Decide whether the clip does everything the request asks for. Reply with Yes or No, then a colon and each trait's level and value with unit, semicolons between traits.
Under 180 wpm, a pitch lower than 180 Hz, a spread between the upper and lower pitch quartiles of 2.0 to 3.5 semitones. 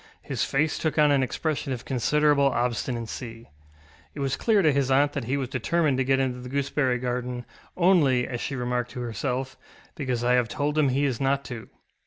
No: average, 200 wpm; low, 135 Hz; narrow, 2.6 semitones